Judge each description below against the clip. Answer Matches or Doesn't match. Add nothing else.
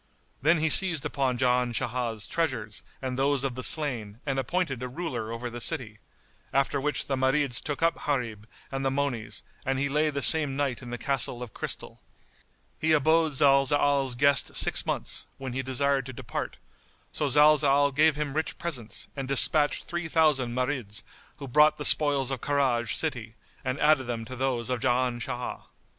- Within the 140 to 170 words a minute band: Doesn't match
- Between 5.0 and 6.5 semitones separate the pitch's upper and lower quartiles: Doesn't match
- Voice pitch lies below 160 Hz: Matches